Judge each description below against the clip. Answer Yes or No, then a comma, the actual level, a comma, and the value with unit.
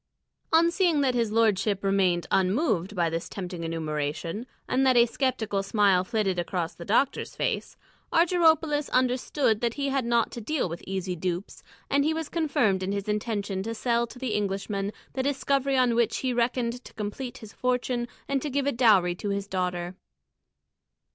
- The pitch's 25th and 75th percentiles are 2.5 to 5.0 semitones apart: No, wide, 5.4 semitones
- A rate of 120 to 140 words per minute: No, average, 175 wpm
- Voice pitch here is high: Yes, high, 225 Hz